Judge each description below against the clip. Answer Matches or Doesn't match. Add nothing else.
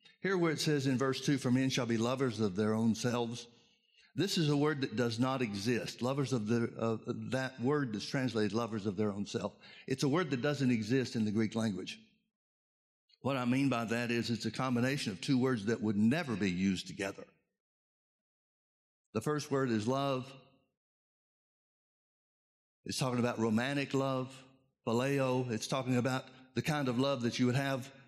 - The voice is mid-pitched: Doesn't match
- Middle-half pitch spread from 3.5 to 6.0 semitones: Doesn't match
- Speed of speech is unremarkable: Matches